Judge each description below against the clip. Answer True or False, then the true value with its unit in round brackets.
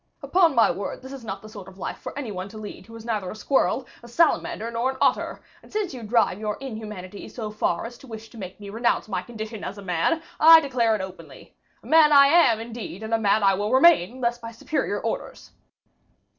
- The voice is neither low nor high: False (225 Hz)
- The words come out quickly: True (235 wpm)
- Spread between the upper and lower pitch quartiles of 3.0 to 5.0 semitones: True (4.0 semitones)